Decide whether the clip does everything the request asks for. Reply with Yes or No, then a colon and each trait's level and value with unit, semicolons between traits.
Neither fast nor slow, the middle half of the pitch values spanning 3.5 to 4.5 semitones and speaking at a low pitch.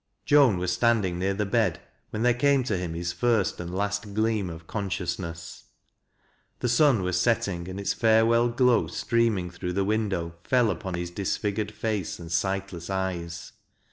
Yes: average, 165 wpm; average, 4.2 semitones; low, 100 Hz